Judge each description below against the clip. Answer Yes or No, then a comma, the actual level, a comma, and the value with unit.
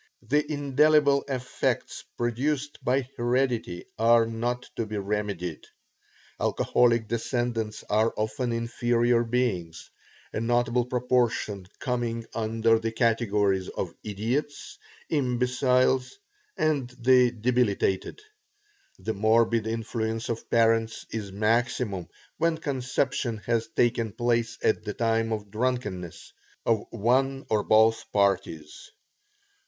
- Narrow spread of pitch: Yes, narrow, 2.3 semitones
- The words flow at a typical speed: No, slow, 105 wpm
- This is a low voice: Yes, low, 115 Hz